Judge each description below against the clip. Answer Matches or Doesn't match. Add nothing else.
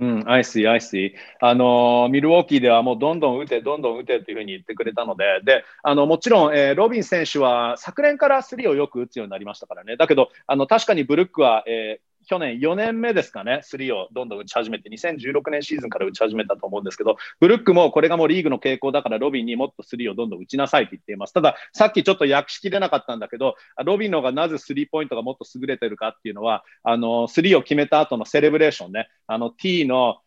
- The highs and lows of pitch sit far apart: Matches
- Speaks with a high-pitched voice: Doesn't match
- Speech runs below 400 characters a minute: Doesn't match